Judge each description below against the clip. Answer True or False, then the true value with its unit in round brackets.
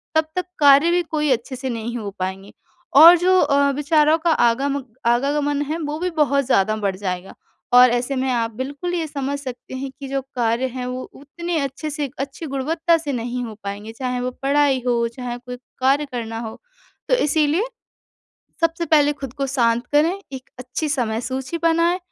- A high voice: True (275 Hz)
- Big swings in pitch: False (3.8 semitones)